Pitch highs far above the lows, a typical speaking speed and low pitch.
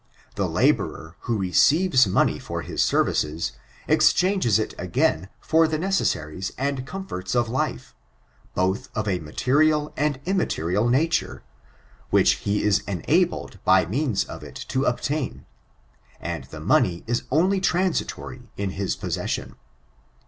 No: wide, 8.6 semitones; slow, 130 wpm; low, 125 Hz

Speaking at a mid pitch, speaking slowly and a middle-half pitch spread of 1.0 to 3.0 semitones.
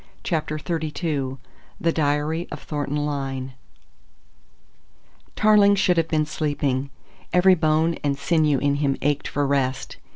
Yes: medium, 150 Hz; slow, 125 wpm; narrow, 2.6 semitones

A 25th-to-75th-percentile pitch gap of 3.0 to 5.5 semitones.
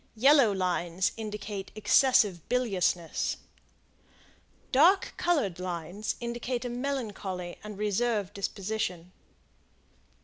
Yes: average, 4.7 semitones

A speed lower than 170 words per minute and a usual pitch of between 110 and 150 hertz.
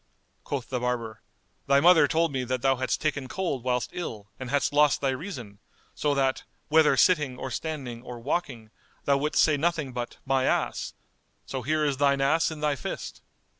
No: average, 185 wpm; low, 135 Hz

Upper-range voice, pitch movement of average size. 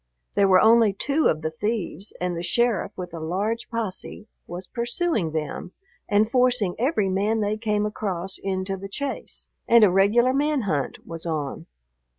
Yes: high, 205 Hz; average, 4.3 semitones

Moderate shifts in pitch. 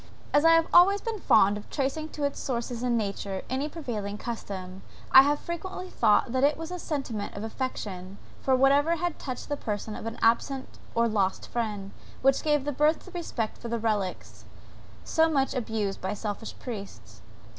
No: wide, 5.9 semitones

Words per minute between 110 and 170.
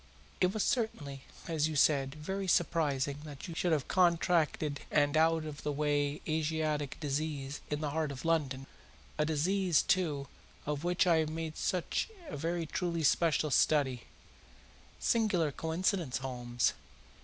Yes: average, 145 wpm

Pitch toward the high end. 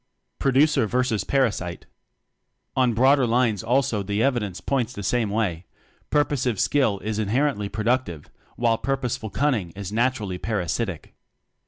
No: low, 115 Hz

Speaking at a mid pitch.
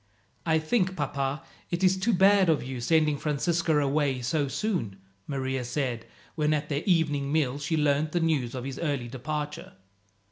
Yes: medium, 150 Hz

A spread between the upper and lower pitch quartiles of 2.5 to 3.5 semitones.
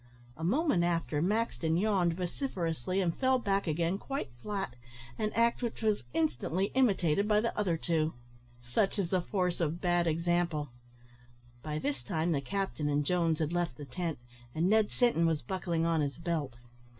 No: average, 4.0 semitones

